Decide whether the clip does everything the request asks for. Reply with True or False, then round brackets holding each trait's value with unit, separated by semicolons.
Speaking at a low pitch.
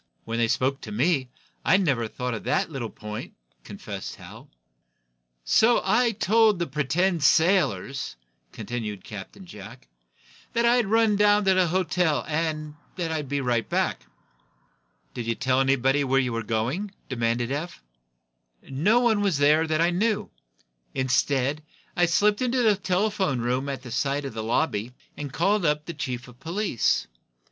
False (150 Hz)